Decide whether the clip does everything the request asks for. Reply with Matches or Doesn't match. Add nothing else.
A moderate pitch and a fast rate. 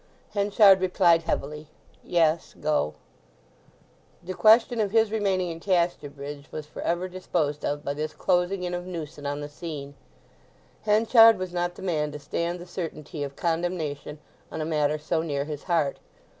Doesn't match